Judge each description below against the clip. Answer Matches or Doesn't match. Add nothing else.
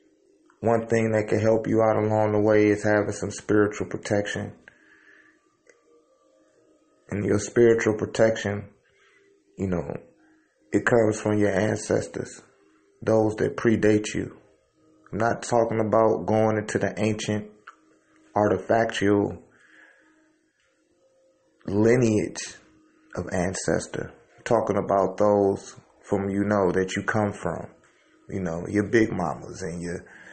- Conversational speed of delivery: Doesn't match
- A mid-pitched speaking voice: Doesn't match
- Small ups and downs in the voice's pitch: Matches